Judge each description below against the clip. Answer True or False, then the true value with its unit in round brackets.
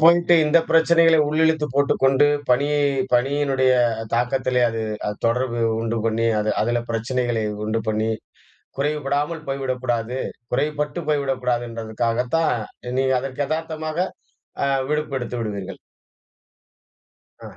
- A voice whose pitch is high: False (130 Hz)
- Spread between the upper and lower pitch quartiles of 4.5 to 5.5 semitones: False (4.1 semitones)